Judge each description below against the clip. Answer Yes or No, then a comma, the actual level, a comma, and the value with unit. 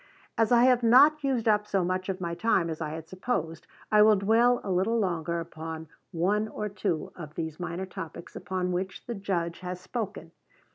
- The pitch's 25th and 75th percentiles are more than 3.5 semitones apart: Yes, average, 4.4 semitones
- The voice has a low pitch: No, medium, 185 Hz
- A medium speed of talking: Yes, average, 195 wpm